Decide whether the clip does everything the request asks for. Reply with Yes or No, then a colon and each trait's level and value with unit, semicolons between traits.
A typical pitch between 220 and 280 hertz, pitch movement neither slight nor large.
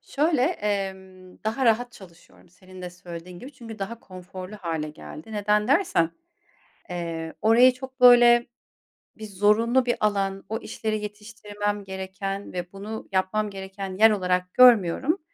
No: high, 205 Hz; average, 3.6 semitones